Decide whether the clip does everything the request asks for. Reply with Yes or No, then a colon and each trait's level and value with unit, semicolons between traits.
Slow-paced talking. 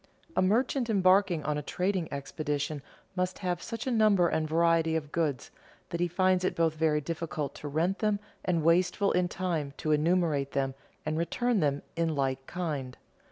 No: average, 175 wpm